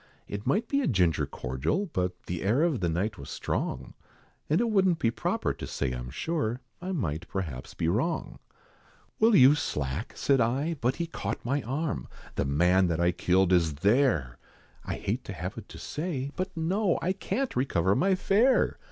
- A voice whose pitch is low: Yes, low, 115 Hz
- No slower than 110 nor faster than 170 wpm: No, average, 185 wpm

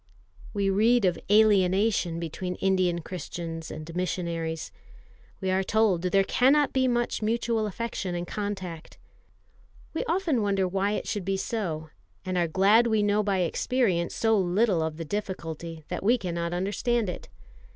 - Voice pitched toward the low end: No, high, 190 Hz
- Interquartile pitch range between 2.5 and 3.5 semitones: No, average, 3.9 semitones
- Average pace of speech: Yes, average, 150 wpm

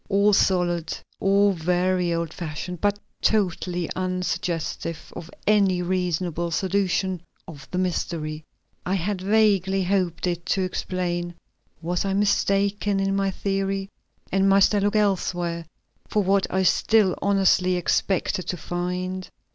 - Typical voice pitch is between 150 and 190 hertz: Yes, medium, 185 Hz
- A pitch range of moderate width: No, narrow, 2.0 semitones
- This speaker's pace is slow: Yes, slow, 130 wpm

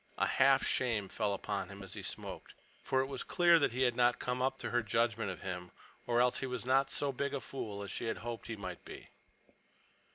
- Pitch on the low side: Yes, low, 120 Hz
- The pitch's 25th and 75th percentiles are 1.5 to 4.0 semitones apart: No, average, 4.4 semitones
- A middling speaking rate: No, fast, 230 wpm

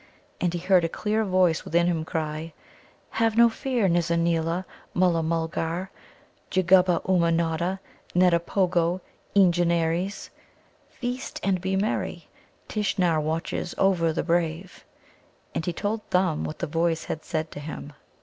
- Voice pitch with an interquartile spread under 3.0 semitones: Yes, narrow, 2.4 semitones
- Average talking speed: No, slow, 130 wpm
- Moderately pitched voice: Yes, medium, 175 Hz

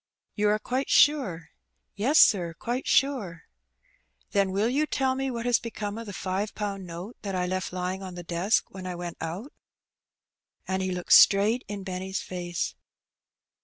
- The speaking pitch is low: No, high, 195 Hz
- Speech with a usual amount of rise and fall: Yes, average, 4.1 semitones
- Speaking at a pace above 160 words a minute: Yes, average, 170 wpm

